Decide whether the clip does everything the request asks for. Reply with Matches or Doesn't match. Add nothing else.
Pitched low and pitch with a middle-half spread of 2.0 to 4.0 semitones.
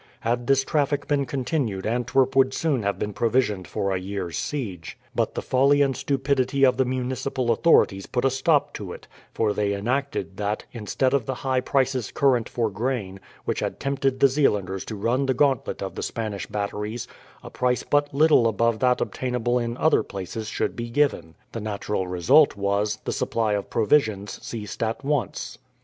Doesn't match